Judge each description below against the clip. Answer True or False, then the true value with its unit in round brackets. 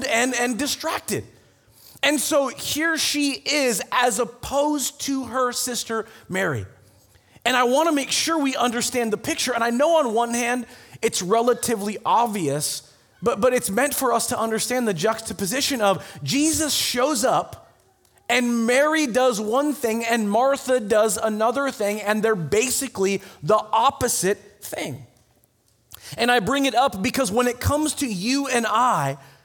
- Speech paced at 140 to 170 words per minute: True (155 wpm)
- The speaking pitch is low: False (240 Hz)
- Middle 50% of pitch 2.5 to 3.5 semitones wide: False (4.0 semitones)